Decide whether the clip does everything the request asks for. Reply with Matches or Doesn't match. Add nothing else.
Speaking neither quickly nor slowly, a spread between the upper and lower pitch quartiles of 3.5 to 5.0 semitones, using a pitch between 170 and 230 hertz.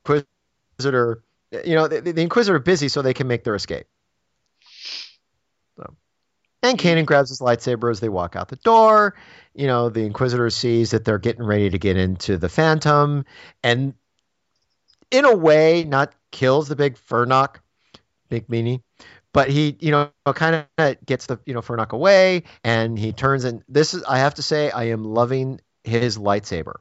Doesn't match